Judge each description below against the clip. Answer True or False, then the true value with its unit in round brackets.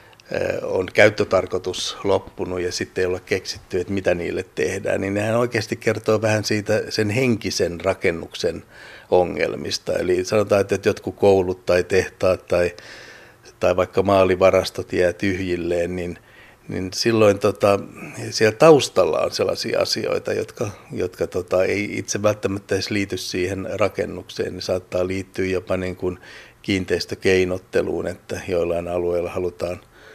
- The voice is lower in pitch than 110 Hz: True (95 Hz)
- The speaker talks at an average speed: True (130 wpm)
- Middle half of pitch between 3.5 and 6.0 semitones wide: False (3.1 semitones)